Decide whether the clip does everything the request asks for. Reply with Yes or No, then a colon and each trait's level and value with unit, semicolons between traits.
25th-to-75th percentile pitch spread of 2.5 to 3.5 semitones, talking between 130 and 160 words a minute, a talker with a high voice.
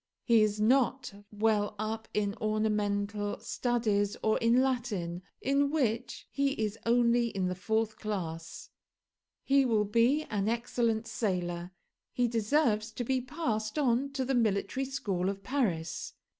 Yes: average, 3.2 semitones; average, 140 wpm; high, 220 Hz